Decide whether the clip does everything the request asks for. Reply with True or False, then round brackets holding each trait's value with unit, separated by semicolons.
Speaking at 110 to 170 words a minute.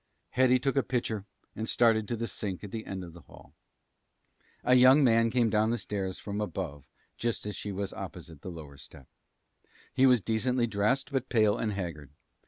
False (190 wpm)